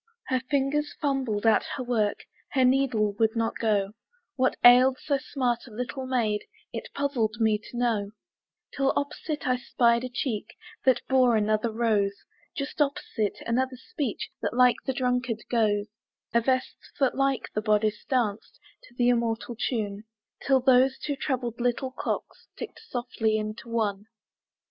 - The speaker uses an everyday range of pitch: Yes, average, 3.1 semitones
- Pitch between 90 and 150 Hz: No, high, 245 Hz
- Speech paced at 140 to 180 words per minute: Yes, average, 155 wpm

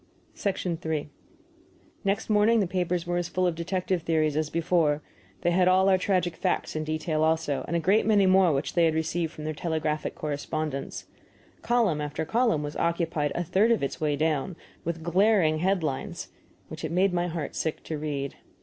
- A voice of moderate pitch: Yes, medium, 170 Hz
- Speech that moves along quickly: No, average, 185 wpm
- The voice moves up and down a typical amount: Yes, average, 3.1 semitones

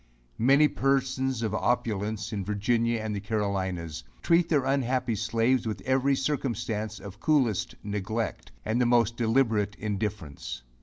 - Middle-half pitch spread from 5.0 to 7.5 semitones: No, average, 3.9 semitones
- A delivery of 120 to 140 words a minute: Yes, slow, 135 wpm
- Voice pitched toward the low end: Yes, low, 115 Hz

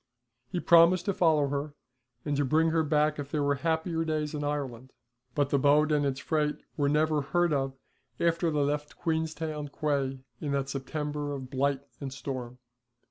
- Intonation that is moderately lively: No, narrow, 2.1 semitones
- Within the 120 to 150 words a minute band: No, average, 175 wpm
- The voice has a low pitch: No, medium, 150 Hz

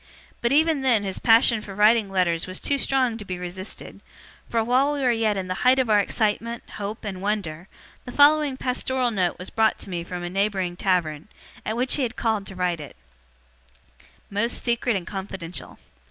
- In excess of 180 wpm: Yes, average, 195 wpm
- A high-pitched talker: Yes, high, 210 Hz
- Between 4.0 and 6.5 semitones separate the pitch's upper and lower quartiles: Yes, average, 4.7 semitones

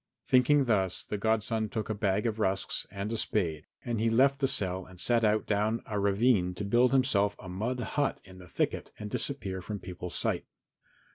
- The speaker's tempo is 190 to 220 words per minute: Yes, average, 200 wpm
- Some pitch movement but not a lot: Yes, average, 3.5 semitones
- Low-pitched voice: Yes, low, 105 Hz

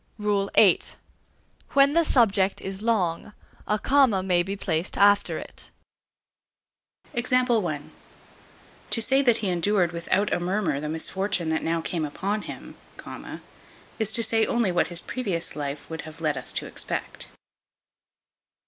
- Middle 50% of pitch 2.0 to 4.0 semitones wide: No, average, 4.7 semitones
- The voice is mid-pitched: No, high, 195 Hz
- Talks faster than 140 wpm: No, slow, 135 wpm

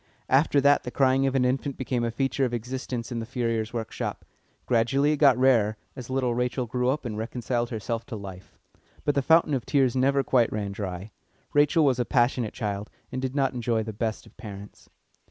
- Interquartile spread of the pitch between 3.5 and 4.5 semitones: No, average, 2.9 semitones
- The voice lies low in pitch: Yes, low, 125 Hz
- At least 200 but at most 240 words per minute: Yes, fast, 205 wpm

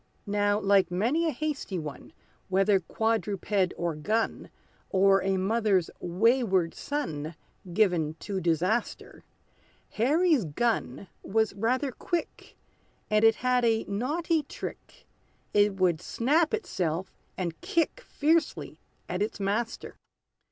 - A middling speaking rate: No, slow, 115 wpm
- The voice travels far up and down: No, average, 4.7 semitones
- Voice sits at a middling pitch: No, high, 205 Hz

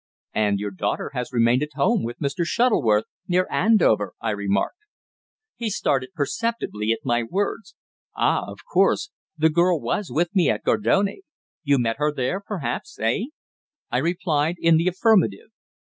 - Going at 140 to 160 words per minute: Yes, average, 155 wpm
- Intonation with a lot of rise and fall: Yes, wide, 8.2 semitones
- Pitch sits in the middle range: Yes, medium, 150 Hz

